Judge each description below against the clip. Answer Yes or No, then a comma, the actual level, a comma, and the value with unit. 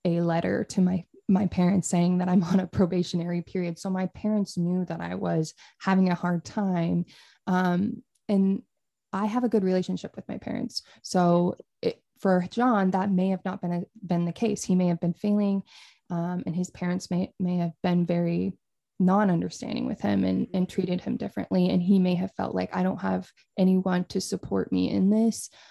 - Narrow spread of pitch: Yes, narrow, 2.0 semitones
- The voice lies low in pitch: No, medium, 185 Hz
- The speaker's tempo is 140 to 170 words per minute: No, average, 200 wpm